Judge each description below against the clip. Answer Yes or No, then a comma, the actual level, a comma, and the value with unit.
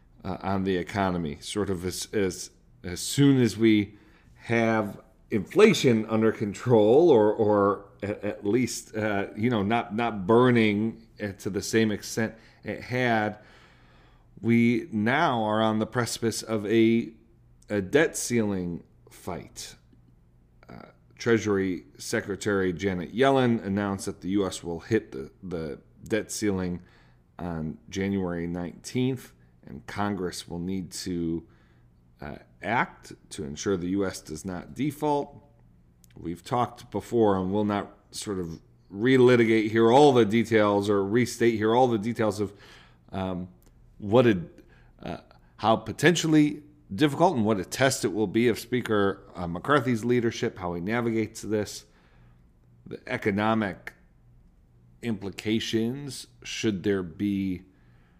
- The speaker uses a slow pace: Yes, slow, 130 wpm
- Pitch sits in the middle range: No, low, 105 Hz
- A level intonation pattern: No, average, 4.2 semitones